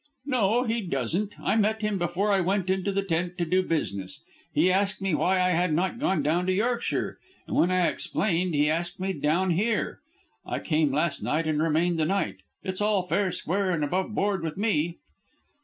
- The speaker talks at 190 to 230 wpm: Yes, average, 195 wpm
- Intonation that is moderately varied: Yes, average, 3.3 semitones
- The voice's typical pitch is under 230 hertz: Yes, medium, 185 Hz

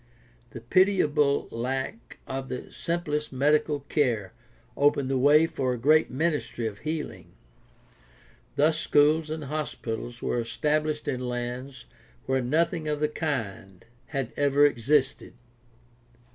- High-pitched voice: No, medium, 140 Hz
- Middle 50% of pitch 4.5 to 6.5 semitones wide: No, average, 3.5 semitones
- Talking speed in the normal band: No, slow, 120 wpm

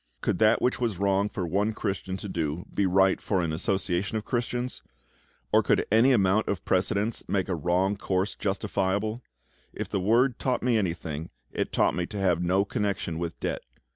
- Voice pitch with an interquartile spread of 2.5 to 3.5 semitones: Yes, average, 3.0 semitones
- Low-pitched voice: Yes, very low, 95 Hz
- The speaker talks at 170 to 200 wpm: Yes, average, 185 wpm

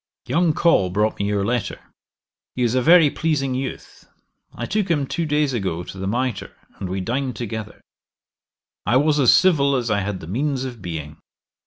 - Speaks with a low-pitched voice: Yes, low, 125 Hz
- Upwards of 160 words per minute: Yes, average, 185 wpm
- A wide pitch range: Yes, wide, 6.3 semitones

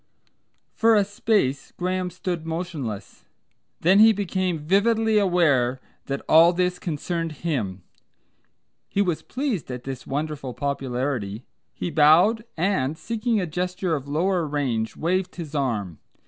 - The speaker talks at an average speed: No, slow, 130 wpm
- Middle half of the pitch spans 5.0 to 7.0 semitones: Yes, average, 5.3 semitones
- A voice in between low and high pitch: Yes, medium, 165 Hz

